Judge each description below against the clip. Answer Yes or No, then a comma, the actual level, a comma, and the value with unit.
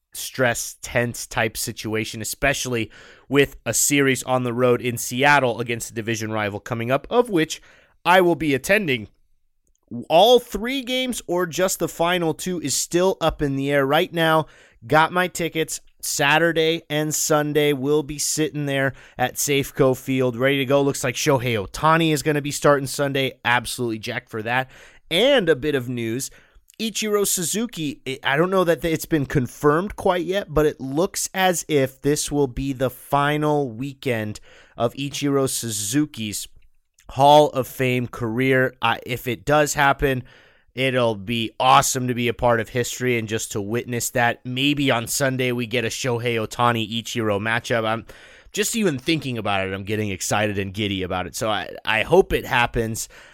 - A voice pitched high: No, low, 135 Hz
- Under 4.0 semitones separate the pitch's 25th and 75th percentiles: No, average, 4.3 semitones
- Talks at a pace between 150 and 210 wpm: Yes, average, 170 wpm